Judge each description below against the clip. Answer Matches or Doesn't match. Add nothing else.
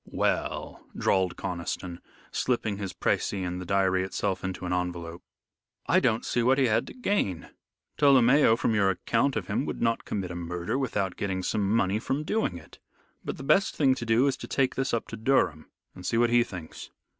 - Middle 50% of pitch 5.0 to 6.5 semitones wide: Matches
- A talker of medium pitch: Doesn't match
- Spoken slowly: Doesn't match